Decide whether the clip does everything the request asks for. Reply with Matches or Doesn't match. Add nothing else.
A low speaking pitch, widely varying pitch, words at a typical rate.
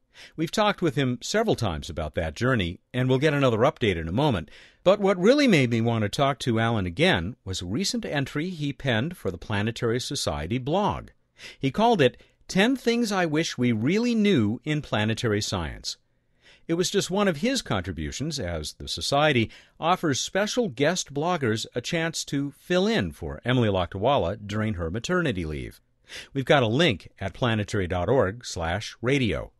Matches